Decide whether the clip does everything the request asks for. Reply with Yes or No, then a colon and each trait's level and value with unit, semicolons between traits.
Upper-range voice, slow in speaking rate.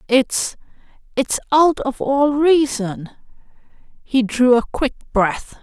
Yes: very high, 255 Hz; slow, 105 wpm